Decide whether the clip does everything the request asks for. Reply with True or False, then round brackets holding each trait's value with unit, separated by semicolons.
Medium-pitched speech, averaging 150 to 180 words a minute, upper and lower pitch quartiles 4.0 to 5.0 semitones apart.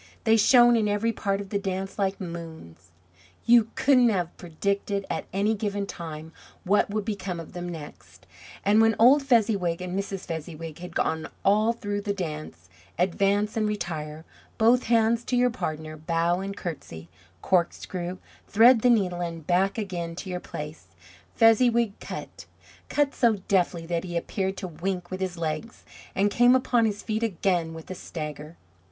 False (195 Hz; 165 wpm; 4.4 semitones)